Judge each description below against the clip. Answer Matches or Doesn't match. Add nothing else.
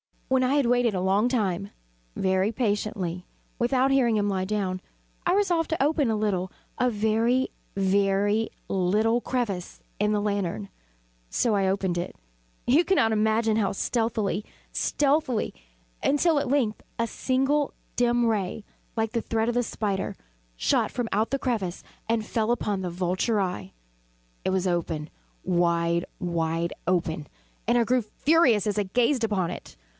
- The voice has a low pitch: Doesn't match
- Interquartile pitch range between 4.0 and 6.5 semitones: Matches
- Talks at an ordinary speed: Matches